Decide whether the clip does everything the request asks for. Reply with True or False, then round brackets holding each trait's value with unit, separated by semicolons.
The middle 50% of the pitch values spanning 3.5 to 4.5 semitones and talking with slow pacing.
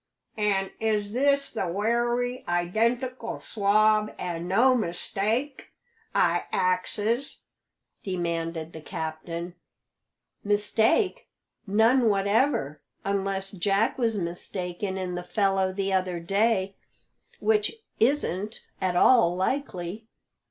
True (4.1 semitones; 95 wpm)